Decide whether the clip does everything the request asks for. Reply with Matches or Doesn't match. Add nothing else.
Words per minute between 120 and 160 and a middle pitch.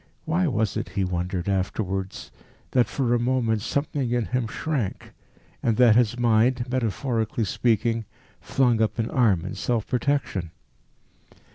Doesn't match